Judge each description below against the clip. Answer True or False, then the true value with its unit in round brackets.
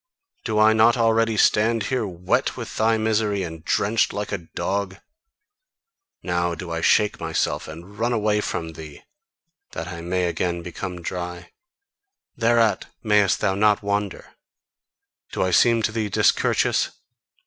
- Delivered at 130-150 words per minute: True (145 wpm)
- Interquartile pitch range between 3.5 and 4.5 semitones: True (3.9 semitones)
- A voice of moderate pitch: False (100 Hz)